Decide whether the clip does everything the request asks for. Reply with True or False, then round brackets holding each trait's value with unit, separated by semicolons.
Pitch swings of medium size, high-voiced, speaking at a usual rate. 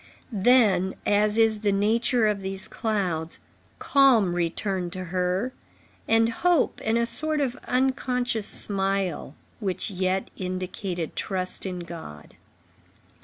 False (4.0 semitones; 200 Hz; 120 wpm)